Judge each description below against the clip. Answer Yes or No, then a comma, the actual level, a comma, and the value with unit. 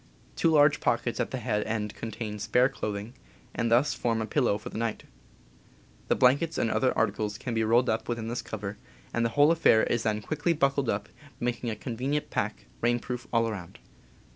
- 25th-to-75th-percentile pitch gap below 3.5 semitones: Yes, average, 3.0 semitones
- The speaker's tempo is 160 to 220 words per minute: Yes, average, 195 wpm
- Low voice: Yes, low, 115 Hz